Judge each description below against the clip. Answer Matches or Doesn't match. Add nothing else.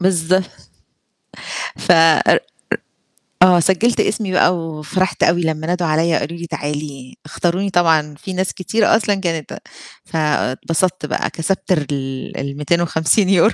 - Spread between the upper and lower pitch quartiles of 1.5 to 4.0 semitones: Matches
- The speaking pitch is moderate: Matches